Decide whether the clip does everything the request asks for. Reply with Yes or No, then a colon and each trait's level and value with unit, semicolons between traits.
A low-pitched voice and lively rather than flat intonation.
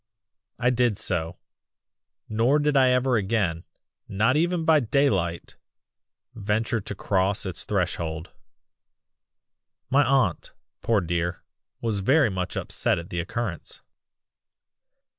Yes: low, 105 Hz; wide, 5.9 semitones